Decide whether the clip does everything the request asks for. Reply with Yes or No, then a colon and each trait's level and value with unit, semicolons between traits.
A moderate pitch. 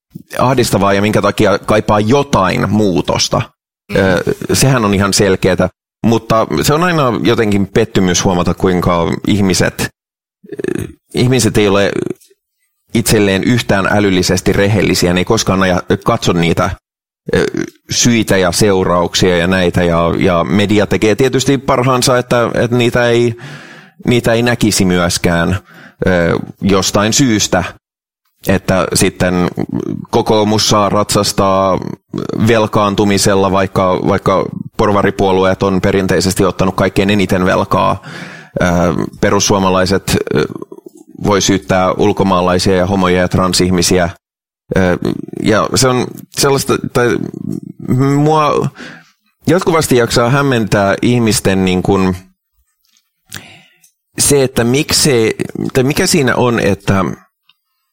No: low, 100 Hz